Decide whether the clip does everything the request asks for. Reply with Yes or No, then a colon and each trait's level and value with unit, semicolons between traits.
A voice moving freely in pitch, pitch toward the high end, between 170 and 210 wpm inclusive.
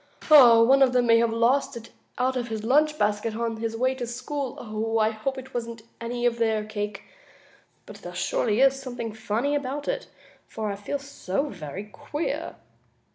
No: average, 3.3 semitones; high, 235 Hz; average, 180 wpm